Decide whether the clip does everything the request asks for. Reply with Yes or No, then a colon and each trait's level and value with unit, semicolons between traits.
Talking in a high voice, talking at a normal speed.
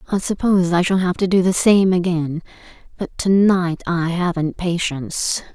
No: medium, 180 Hz; average, 175 wpm